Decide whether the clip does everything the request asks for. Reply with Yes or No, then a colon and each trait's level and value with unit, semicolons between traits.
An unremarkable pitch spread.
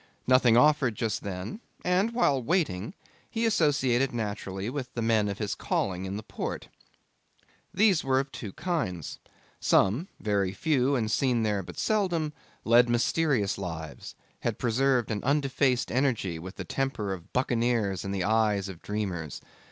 No: wide, 5.7 semitones